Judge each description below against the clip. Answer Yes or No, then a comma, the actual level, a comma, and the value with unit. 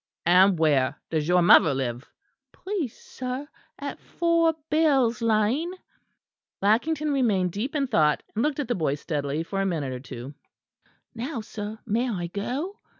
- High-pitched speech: Yes, high, 215 Hz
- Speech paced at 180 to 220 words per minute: No, average, 150 wpm